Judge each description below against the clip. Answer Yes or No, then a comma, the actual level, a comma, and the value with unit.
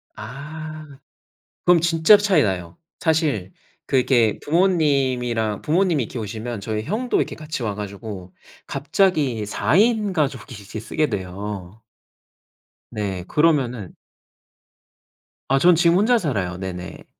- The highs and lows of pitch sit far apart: Yes, wide, 7.4 semitones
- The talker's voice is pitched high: No, low, 130 Hz